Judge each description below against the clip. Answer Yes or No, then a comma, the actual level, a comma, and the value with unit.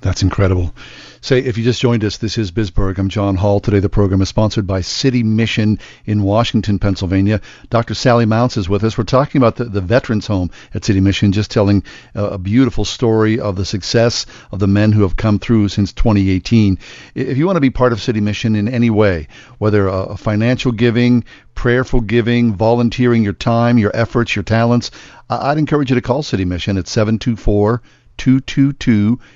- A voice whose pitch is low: Yes, low, 110 Hz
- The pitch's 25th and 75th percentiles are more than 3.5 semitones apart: No, average, 2.9 semitones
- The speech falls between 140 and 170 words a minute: No, average, 195 wpm